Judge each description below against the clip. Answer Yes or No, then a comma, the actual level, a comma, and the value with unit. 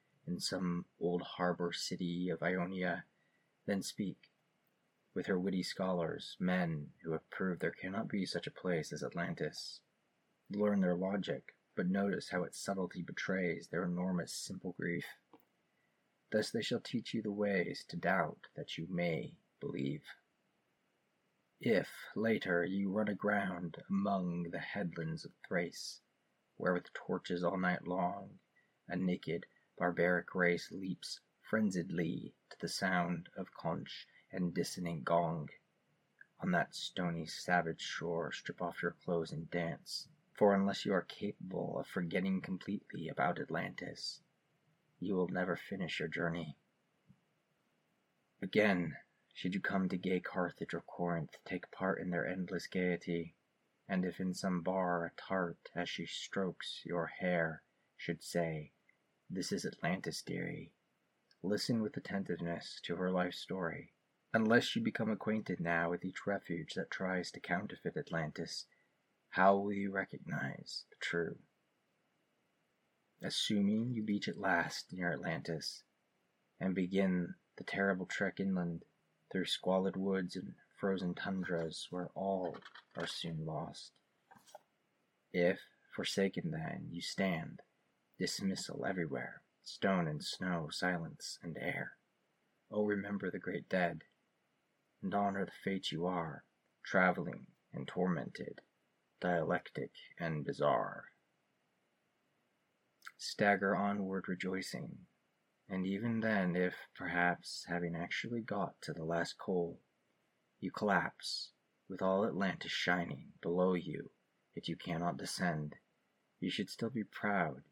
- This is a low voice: Yes, very low, 90 Hz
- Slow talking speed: Yes, slow, 130 wpm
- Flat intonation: Yes, narrow, 2.0 semitones